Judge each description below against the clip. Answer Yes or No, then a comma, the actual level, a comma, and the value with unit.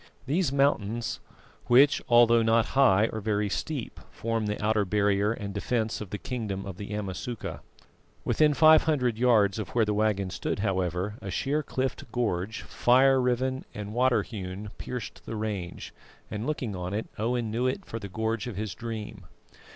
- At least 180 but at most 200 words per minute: No, average, 170 wpm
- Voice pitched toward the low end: Yes, low, 110 Hz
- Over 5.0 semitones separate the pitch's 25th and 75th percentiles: No, average, 3.4 semitones